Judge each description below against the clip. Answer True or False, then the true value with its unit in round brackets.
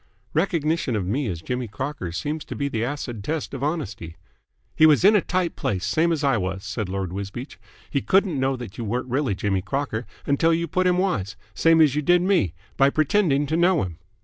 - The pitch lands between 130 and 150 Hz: True (140 Hz)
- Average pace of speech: False (215 wpm)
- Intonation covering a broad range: True (7.9 semitones)